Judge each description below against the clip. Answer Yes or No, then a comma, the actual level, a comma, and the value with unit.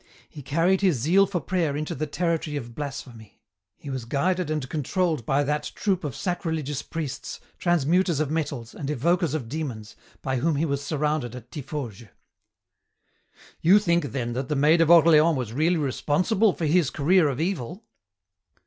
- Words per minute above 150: Yes, average, 165 wpm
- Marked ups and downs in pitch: No, average, 3.8 semitones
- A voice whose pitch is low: No, medium, 150 Hz